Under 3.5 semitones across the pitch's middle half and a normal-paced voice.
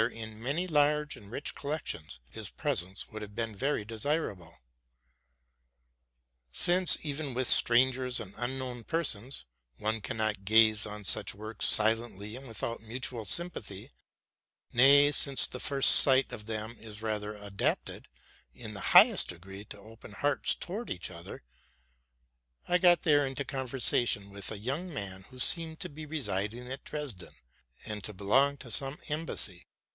No: average, 5.2 semitones; average, 150 wpm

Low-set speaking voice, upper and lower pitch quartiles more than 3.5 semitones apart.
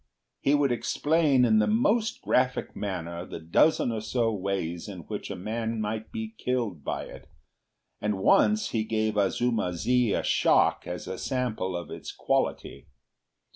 Yes: low, 110 Hz; average, 4.9 semitones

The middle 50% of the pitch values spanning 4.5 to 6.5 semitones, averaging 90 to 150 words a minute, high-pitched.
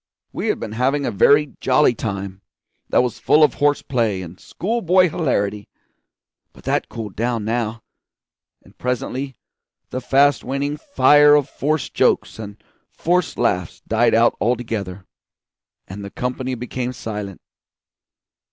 No: average, 5.1 semitones; average, 140 wpm; low, 125 Hz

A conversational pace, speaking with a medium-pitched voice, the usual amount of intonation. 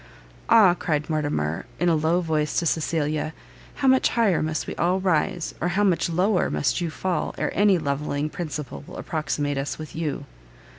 Yes: average, 180 wpm; medium, 160 Hz; average, 3.0 semitones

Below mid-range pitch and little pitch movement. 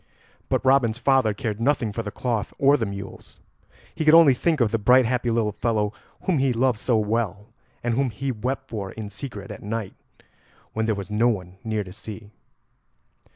No: low, 115 Hz; average, 3.7 semitones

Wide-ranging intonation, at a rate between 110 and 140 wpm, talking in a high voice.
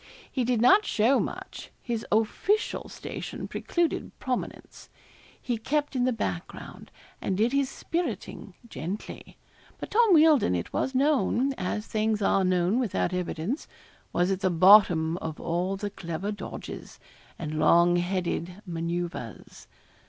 Yes: wide, 6.5 semitones; slow, 135 wpm; high, 205 Hz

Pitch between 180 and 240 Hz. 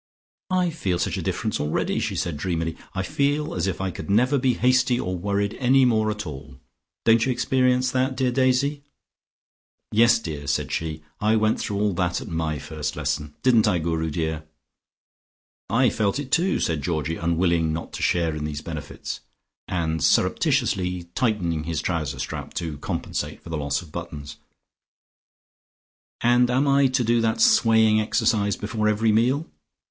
No: low, 100 Hz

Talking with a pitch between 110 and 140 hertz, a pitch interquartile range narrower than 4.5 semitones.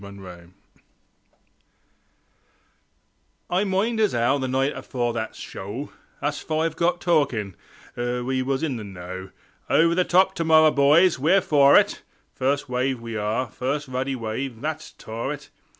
No: low, 135 Hz; average, 5.2 semitones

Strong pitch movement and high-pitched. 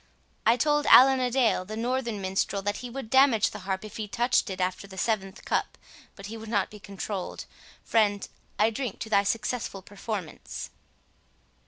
No: average, 3.5 semitones; high, 215 Hz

